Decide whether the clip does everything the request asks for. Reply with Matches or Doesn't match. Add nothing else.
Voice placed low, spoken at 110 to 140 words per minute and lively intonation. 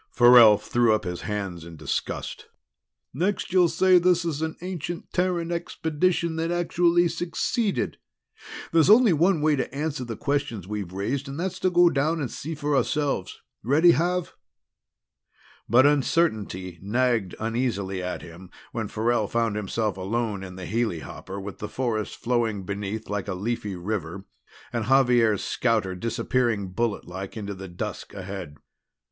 Doesn't match